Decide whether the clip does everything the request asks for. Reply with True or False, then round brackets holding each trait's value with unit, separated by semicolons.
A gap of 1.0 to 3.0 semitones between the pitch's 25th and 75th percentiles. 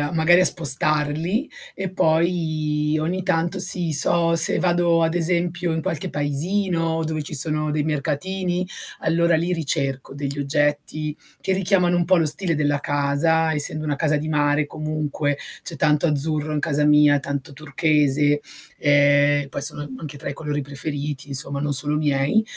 True (2.4 semitones)